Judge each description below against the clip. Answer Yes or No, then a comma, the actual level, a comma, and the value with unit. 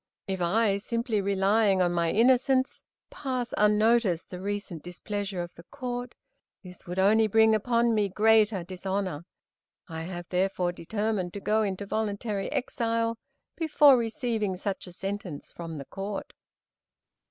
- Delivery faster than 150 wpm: No, average, 140 wpm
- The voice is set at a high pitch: Yes, high, 205 Hz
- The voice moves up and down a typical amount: Yes, average, 3.6 semitones